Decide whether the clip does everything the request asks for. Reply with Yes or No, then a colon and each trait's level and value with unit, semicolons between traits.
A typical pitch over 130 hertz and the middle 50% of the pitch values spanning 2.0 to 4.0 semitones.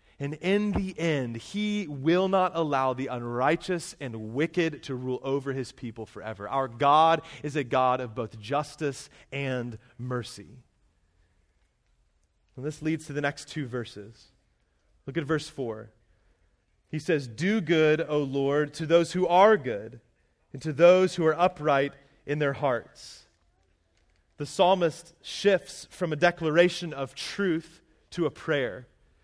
No: medium, 140 Hz; wide, 5.6 semitones